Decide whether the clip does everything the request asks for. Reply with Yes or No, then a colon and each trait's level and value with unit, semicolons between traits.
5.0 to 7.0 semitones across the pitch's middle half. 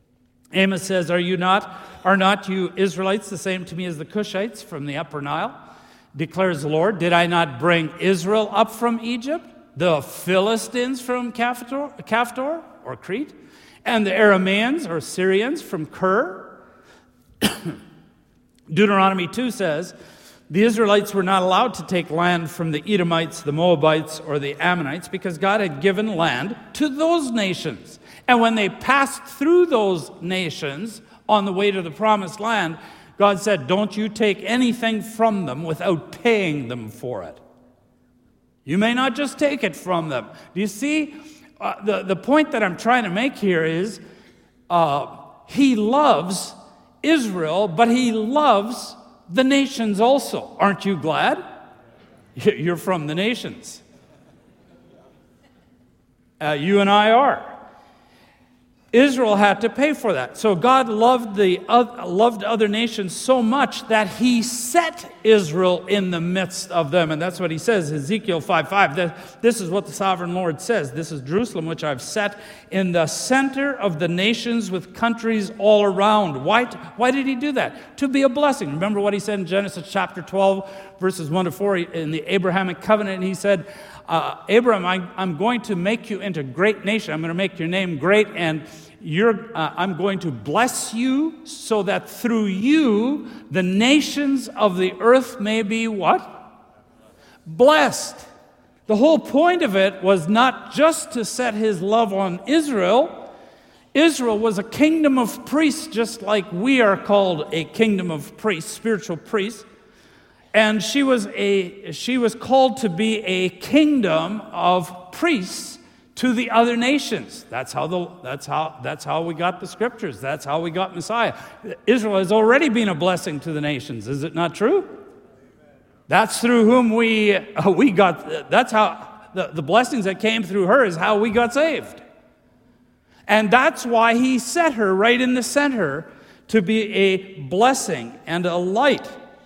No: average, 4.6 semitones